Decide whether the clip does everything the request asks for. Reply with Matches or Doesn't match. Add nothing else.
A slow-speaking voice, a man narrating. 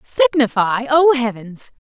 Doesn't match